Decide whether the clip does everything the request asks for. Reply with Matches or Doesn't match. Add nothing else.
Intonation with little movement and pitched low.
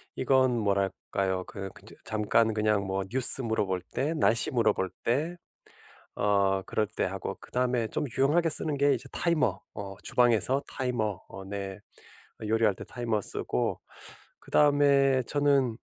Doesn't match